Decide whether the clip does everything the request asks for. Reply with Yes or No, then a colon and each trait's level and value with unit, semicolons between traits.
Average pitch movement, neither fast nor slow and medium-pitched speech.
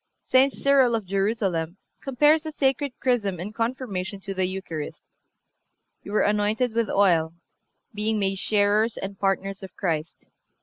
No: average, 3.8 semitones; average, 145 wpm; high, 205 Hz